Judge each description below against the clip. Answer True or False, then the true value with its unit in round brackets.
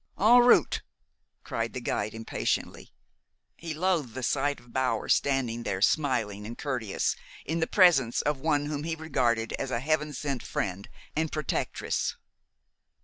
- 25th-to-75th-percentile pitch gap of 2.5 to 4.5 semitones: False (5.0 semitones)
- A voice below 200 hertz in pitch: True (135 Hz)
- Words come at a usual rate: True (145 wpm)